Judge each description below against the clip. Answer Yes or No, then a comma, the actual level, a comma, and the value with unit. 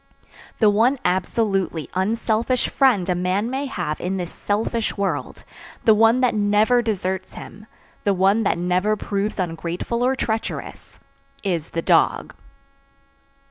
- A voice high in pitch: Yes, high, 205 Hz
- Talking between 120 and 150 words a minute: Yes, slow, 135 wpm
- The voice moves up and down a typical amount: Yes, average, 3.6 semitones